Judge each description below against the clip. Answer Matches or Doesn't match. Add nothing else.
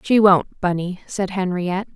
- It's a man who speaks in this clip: Doesn't match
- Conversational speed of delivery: Matches